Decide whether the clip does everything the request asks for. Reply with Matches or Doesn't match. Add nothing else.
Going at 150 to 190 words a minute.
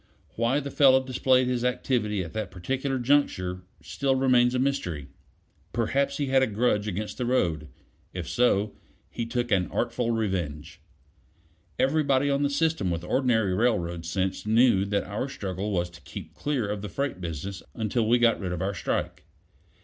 Matches